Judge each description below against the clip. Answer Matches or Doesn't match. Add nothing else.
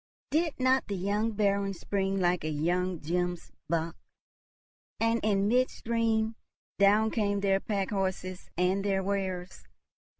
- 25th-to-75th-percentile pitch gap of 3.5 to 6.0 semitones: Doesn't match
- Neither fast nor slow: Doesn't match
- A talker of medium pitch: Doesn't match